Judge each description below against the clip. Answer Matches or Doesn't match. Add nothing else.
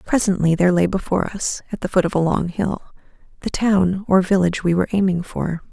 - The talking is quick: Matches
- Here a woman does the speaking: Matches